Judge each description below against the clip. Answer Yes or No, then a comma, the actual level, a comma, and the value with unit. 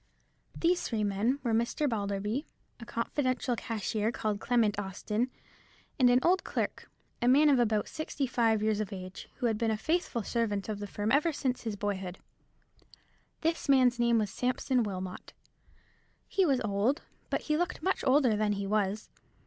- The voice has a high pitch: Yes, high, 230 Hz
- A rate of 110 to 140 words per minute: No, average, 170 wpm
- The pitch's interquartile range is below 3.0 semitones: No, average, 3.9 semitones